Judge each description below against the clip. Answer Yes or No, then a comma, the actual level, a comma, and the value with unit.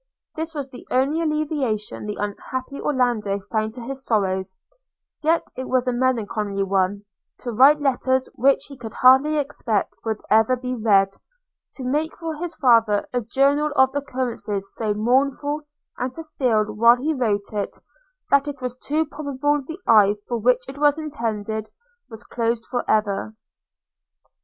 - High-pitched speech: Yes, very high, 250 Hz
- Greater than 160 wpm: No, average, 155 wpm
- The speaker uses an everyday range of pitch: Yes, average, 4.6 semitones